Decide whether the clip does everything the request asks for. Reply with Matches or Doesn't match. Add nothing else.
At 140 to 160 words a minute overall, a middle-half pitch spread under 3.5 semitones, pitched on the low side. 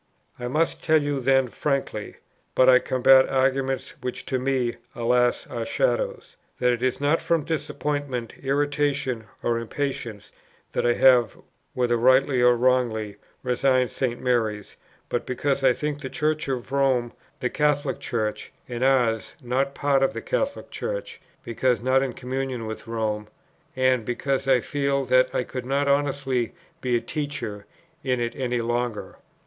Matches